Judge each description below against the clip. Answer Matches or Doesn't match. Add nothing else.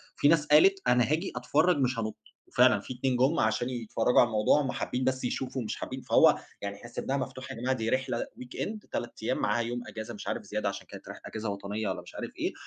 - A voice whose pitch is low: Matches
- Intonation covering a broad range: Doesn't match